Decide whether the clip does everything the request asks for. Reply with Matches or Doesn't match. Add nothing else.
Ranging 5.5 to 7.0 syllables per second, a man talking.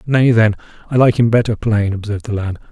Matches